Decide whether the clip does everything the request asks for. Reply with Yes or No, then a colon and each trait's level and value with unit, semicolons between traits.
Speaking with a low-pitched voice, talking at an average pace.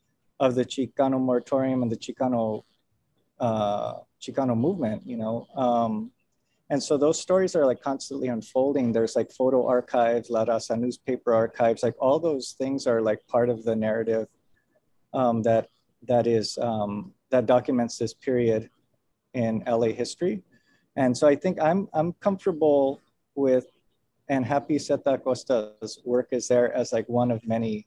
Yes: low, 125 Hz; average, 155 wpm